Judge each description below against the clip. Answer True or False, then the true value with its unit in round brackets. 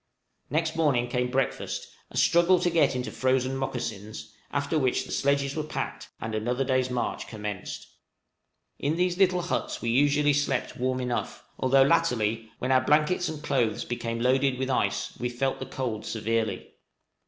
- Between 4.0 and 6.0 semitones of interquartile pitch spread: False (3.1 semitones)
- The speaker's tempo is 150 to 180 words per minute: True (165 wpm)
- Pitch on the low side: True (130 Hz)